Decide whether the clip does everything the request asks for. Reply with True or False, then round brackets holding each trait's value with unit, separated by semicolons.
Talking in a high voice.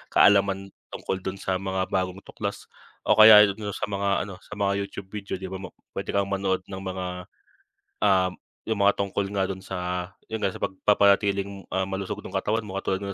False (100 Hz)